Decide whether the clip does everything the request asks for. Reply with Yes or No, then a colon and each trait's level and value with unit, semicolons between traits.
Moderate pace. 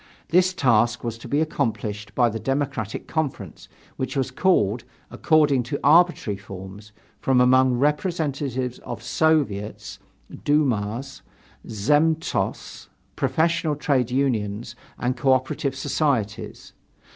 No: slow, 110 wpm